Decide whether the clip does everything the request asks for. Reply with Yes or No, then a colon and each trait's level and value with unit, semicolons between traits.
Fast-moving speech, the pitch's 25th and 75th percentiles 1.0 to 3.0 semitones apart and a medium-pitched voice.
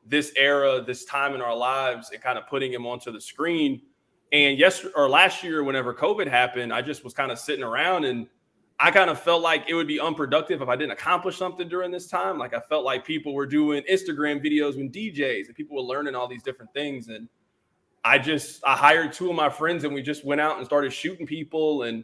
No: fast, 235 wpm; average, 3.5 semitones; medium, 145 Hz